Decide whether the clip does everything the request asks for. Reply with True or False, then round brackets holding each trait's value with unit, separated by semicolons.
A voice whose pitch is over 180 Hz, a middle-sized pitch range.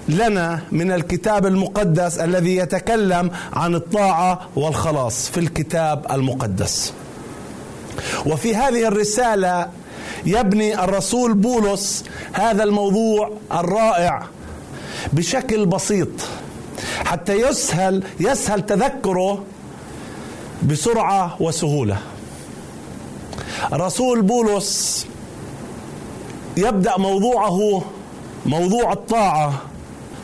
True (190 Hz; 4.1 semitones)